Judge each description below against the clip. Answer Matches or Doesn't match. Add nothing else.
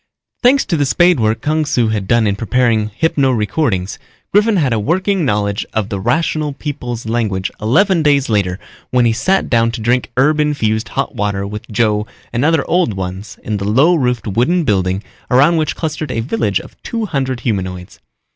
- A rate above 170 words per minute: Matches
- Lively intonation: Matches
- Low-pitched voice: Matches